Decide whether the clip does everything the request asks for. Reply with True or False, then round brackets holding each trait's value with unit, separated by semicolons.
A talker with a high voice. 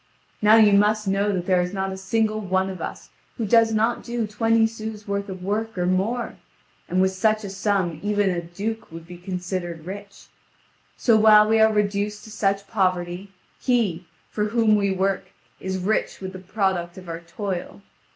True (200 Hz)